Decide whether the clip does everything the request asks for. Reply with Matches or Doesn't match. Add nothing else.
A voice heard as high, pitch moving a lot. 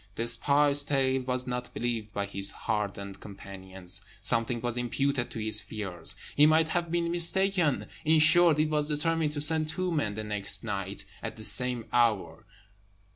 Doesn't match